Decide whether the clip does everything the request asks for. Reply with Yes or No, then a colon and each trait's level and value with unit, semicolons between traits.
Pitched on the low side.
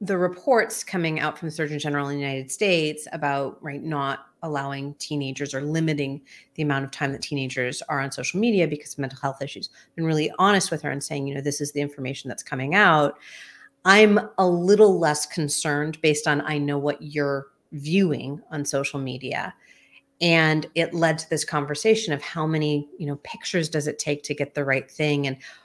No: medium, 150 Hz